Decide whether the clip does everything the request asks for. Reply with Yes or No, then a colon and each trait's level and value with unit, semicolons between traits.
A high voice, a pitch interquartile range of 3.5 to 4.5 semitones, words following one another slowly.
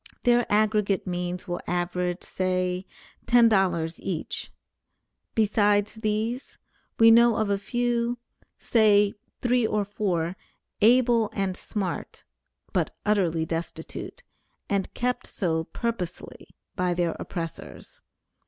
Yes: high, 205 Hz; average, 4.1 semitones; slow, 105 wpm